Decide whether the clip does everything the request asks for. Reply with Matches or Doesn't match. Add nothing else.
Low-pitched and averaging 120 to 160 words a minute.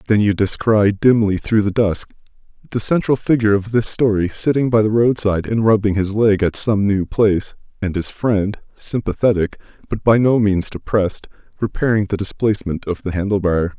Doesn't match